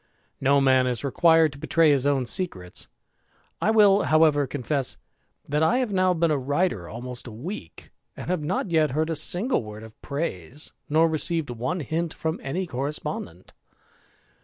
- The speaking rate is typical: Yes, average, 165 wpm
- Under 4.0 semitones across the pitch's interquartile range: No, average, 4.6 semitones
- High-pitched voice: No, medium, 150 Hz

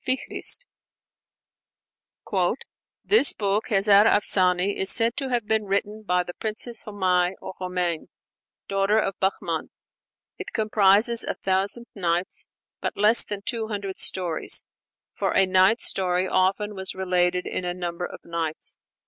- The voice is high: Yes, high, 195 Hz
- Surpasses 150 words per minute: No, average, 140 wpm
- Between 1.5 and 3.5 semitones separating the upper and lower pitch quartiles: Yes, average, 2.8 semitones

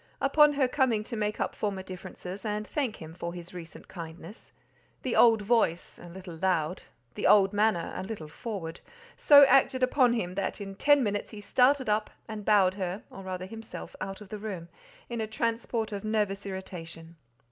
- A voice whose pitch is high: Yes, high, 205 Hz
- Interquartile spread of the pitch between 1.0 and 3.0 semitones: No, average, 3.8 semitones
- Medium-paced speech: Yes, average, 170 wpm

